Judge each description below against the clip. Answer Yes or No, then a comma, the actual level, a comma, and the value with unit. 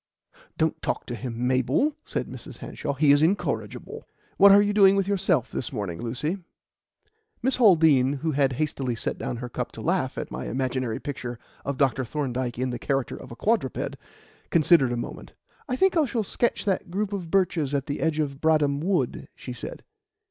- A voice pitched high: No, medium, 145 Hz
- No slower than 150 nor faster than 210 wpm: Yes, average, 190 wpm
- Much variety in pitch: Yes, wide, 6.8 semitones